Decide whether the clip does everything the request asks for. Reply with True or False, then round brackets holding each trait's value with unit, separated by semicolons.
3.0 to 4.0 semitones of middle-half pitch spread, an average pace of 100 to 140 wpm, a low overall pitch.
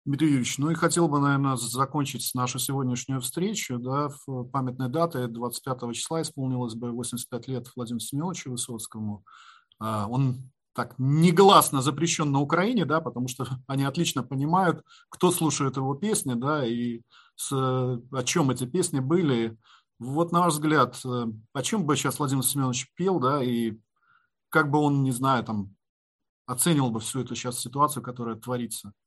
False (3.5 semitones; 155 wpm; 130 Hz)